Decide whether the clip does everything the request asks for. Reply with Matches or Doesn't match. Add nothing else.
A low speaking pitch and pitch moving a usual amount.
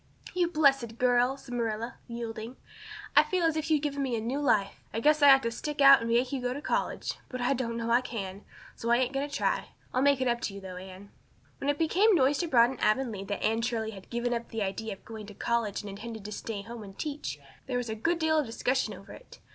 Doesn't match